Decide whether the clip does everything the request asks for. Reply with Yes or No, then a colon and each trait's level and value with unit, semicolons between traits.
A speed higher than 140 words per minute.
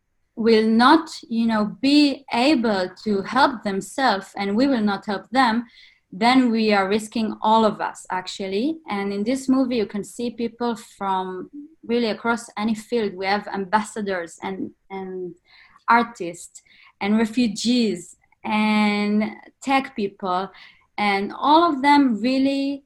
No: slow, 135 wpm